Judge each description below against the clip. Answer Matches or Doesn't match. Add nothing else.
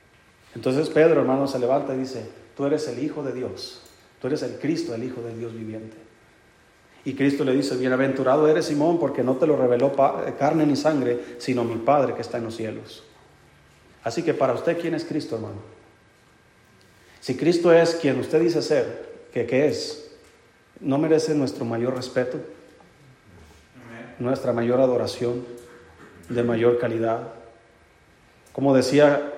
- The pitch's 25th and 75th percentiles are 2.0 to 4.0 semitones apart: Doesn't match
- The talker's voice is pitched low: Matches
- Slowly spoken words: Doesn't match